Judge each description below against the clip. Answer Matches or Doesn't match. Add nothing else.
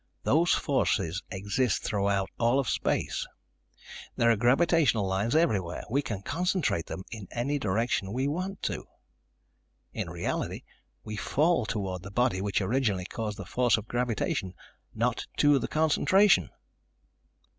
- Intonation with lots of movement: Matches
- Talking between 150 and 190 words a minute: Doesn't match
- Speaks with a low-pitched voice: Matches